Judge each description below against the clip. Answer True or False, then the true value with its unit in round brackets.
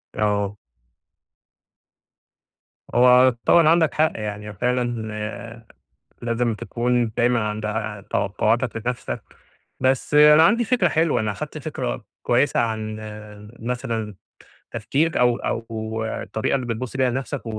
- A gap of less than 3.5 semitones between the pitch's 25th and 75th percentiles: True (3.1 semitones)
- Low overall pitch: True (115 Hz)